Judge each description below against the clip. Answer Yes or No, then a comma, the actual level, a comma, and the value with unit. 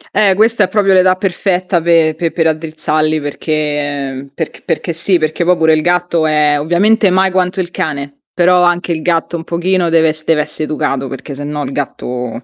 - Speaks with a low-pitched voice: No, medium, 165 Hz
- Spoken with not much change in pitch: No, average, 3.0 semitones